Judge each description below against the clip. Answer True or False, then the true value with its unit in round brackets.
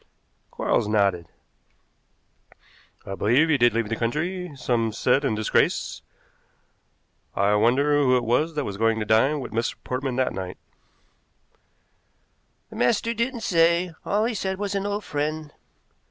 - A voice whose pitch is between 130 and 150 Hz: True (135 Hz)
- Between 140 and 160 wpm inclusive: True (145 wpm)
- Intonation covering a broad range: True (6.9 semitones)